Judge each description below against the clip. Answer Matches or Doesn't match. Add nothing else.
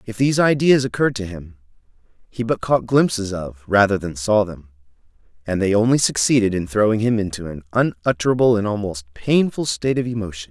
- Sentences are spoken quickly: Doesn't match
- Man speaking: Matches